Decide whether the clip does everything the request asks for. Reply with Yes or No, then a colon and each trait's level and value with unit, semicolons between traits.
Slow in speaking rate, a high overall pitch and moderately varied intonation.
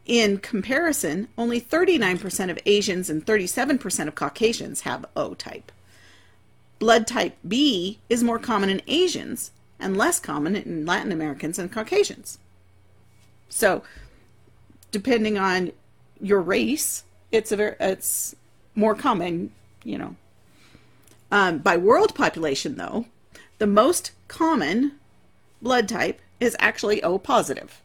Yes: slow, 120 wpm; high, 210 Hz; average, 4.7 semitones